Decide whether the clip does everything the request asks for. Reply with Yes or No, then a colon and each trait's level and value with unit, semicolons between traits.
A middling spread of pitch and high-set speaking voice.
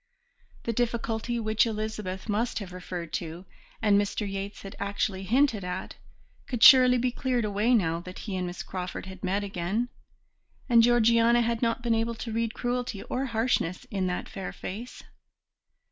Yes: average, 3.8 semitones; high, 215 Hz